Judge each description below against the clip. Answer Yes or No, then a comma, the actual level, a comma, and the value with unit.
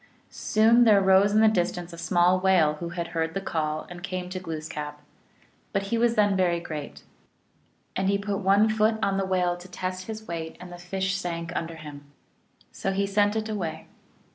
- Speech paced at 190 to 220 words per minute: Yes, average, 200 wpm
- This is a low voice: No, medium, 185 Hz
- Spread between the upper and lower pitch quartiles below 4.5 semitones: Yes, average, 2.8 semitones